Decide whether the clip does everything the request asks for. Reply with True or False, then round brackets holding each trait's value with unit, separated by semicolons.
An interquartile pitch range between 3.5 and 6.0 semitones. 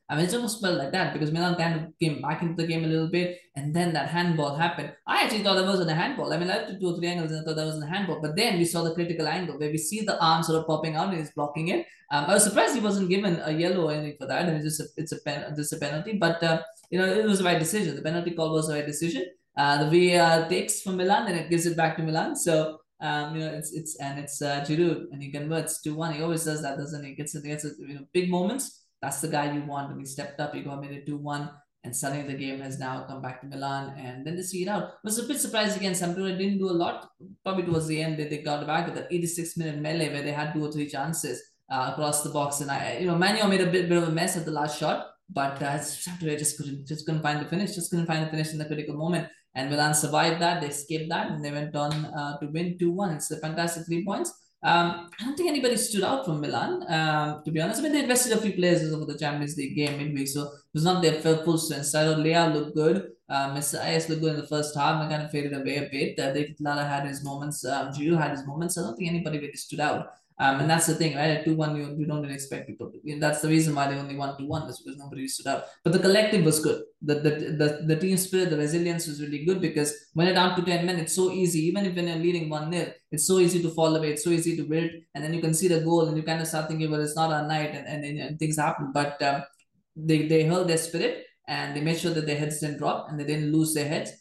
False (2.6 semitones)